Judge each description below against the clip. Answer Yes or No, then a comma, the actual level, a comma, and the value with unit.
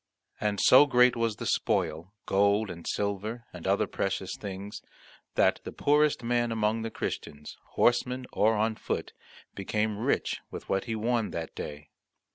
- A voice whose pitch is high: No, low, 110 Hz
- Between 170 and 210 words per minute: No, average, 155 wpm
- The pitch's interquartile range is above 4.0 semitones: No, average, 3.4 semitones